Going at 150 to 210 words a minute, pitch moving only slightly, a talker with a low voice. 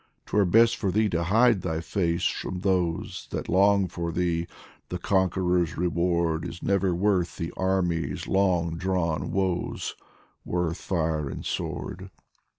No: average, 140 wpm; narrow, 2.3 semitones; very low, 90 Hz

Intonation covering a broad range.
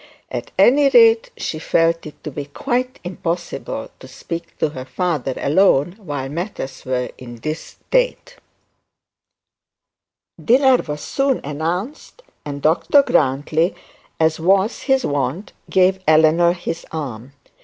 Yes: wide, 6.7 semitones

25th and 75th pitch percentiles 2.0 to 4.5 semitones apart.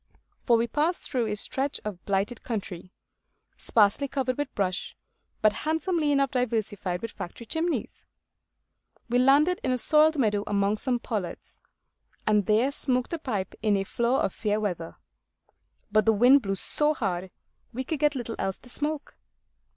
No: average, 5.2 semitones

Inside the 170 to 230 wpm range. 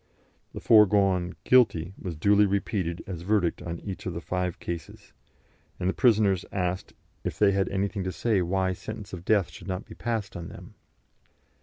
Yes: average, 175 wpm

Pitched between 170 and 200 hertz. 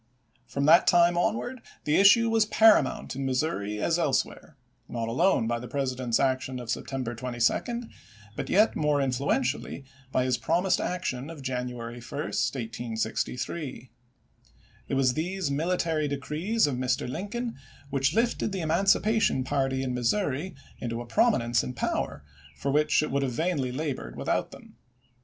No: medium, 140 Hz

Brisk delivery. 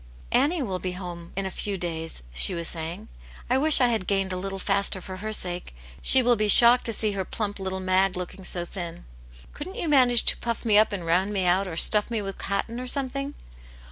Yes: fast, 240 wpm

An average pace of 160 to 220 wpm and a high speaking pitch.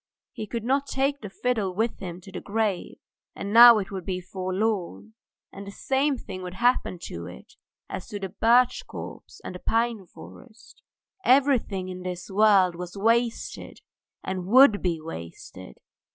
Yes: average, 165 wpm; high, 205 Hz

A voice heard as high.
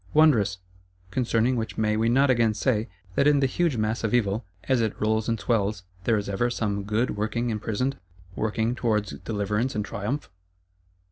No: low, 110 Hz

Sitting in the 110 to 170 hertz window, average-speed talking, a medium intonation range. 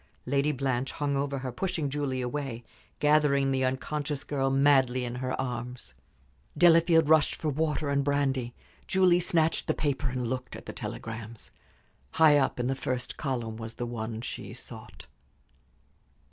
Yes: low, 135 Hz; average, 155 wpm; average, 3.0 semitones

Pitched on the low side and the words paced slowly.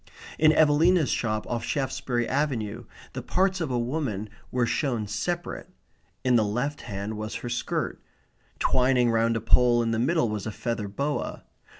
No: low, 120 Hz; average, 165 wpm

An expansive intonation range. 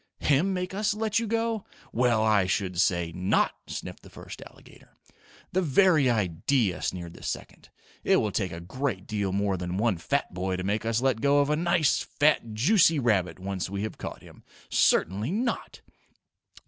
Yes: wide, 8.4 semitones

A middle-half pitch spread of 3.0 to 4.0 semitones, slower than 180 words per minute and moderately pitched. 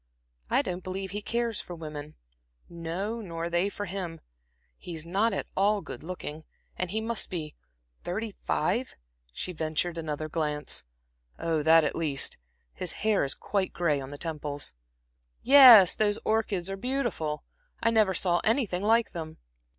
No: average, 4.8 semitones; average, 155 wpm; medium, 180 Hz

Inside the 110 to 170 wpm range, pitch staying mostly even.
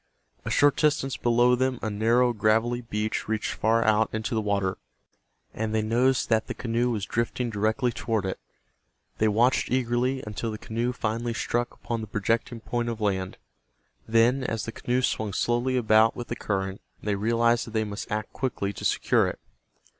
No: average, 180 wpm; narrow, 2.1 semitones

